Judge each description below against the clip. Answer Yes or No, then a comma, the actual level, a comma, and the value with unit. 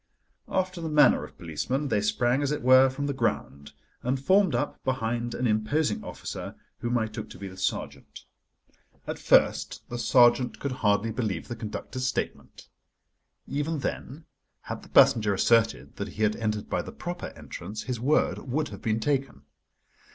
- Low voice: Yes, low, 120 Hz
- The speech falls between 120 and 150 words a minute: No, average, 170 wpm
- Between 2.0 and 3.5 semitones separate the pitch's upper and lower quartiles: No, average, 4.5 semitones